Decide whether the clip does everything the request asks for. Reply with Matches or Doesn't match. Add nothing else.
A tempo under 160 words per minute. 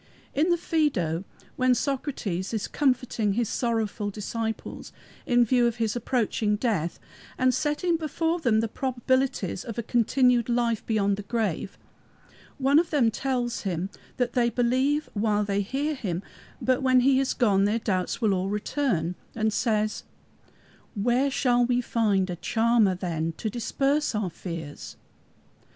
Matches